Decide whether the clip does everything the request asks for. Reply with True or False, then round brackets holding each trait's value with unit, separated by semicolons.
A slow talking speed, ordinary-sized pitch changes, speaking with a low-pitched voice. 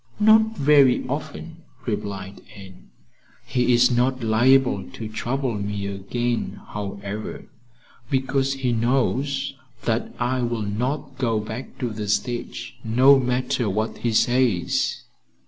True (120 wpm; 3.7 semitones; 120 Hz)